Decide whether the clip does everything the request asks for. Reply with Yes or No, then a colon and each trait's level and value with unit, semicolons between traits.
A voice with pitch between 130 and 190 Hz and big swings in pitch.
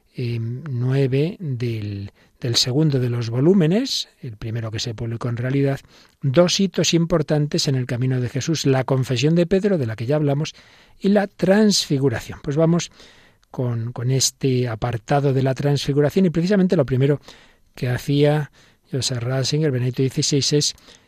No: low, 135 Hz; average, 3.8 semitones